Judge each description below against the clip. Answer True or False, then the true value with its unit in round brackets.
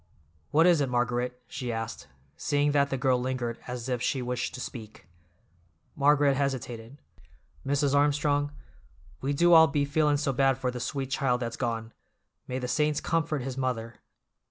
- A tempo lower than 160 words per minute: False (165 wpm)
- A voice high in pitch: False (135 Hz)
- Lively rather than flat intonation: False (2.7 semitones)